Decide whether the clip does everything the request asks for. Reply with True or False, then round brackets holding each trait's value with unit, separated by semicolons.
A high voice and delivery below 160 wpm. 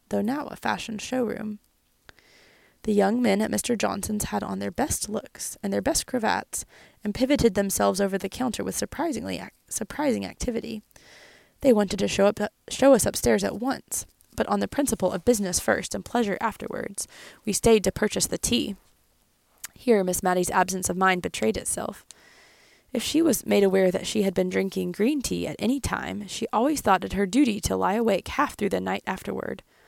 False (210 Hz; 190 wpm)